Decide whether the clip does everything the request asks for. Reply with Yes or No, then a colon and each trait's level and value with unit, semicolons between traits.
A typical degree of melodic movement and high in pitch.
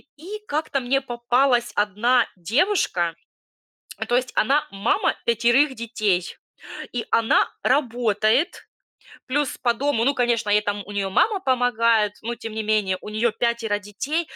Yes: average, 3.8 semitones; high, 235 Hz